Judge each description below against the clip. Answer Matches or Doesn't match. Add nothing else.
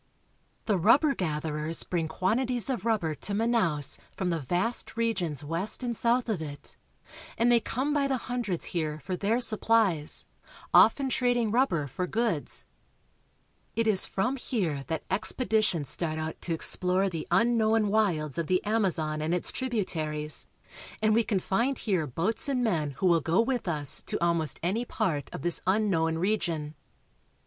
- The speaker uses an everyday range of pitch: Doesn't match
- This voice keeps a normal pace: Matches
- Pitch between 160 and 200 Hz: Matches